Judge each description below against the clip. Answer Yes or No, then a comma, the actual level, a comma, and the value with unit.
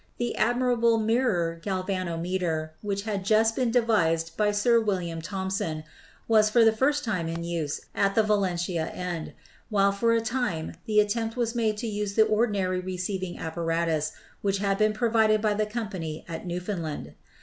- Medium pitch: No, high, 200 Hz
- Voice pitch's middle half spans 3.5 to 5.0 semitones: Yes, average, 4.4 semitones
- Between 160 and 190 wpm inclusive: Yes, average, 165 wpm